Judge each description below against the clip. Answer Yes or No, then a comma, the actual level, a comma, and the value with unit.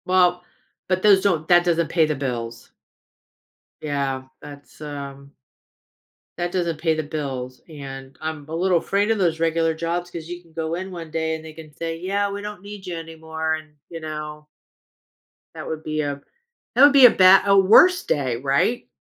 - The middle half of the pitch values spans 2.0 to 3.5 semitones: Yes, average, 3.0 semitones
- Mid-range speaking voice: Yes, medium, 160 Hz